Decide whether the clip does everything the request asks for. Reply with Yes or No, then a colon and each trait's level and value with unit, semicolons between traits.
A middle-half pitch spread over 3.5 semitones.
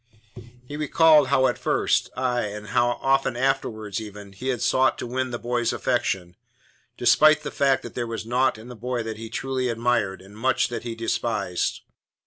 No: average, 2.9 semitones